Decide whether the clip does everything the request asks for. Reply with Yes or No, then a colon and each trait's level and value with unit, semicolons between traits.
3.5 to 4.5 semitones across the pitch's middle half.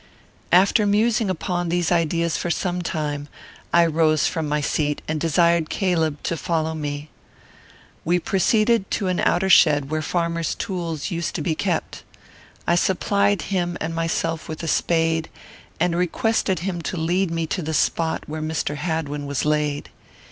No: narrow, 2.4 semitones